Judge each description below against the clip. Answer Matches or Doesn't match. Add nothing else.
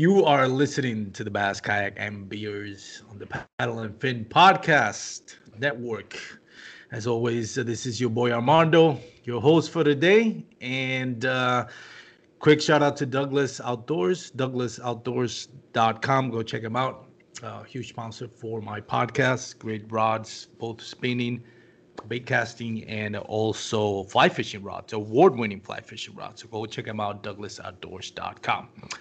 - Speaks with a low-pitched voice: Matches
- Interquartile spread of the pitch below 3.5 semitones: Matches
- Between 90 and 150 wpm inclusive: Matches